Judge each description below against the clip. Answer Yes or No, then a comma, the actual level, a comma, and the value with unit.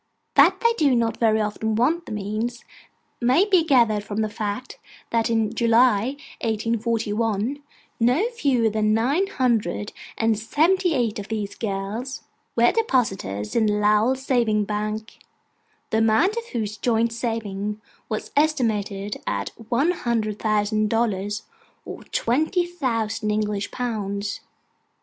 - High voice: Yes, high, 225 Hz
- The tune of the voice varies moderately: Yes, average, 3.1 semitones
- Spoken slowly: Yes, slow, 130 wpm